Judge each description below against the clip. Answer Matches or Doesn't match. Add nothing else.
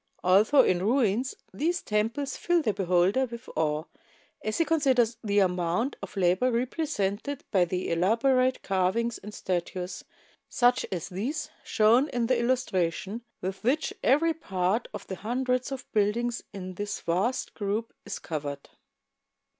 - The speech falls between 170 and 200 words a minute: Doesn't match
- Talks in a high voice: Matches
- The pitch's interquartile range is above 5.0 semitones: Matches